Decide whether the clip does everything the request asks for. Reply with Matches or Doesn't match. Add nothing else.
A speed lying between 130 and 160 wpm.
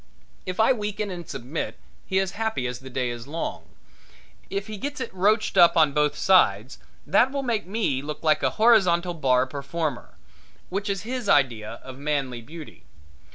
Doesn't match